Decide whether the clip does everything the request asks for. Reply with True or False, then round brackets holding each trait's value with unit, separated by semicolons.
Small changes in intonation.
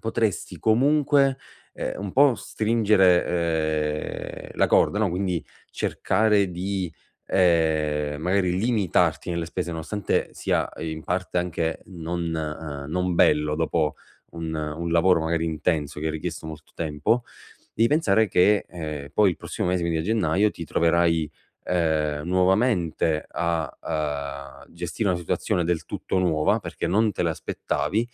False (3.6 semitones)